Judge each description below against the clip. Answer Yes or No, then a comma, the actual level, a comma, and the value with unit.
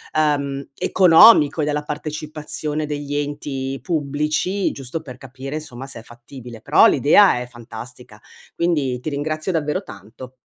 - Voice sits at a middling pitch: Yes, medium, 145 Hz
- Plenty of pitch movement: No, average, 2.8 semitones